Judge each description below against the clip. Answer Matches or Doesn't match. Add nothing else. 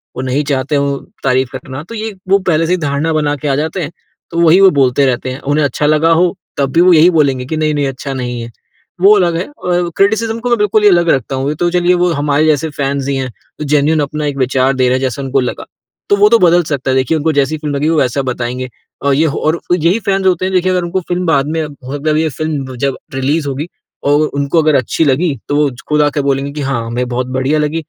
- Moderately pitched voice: Matches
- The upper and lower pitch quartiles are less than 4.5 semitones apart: Matches